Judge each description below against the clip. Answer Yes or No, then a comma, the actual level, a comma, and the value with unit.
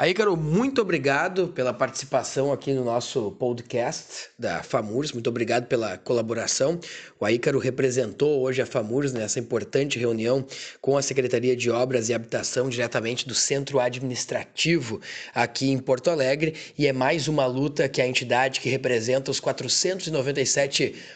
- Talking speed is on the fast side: No, average, 145 wpm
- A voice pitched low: Yes, low, 130 Hz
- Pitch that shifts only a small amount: Yes, narrow, 2.2 semitones